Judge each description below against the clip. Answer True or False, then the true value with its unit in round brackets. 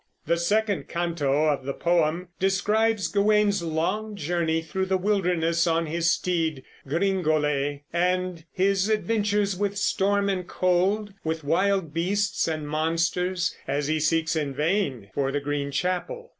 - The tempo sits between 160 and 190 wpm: False (140 wpm)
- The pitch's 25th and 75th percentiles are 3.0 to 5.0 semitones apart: True (3.9 semitones)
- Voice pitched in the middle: True (175 Hz)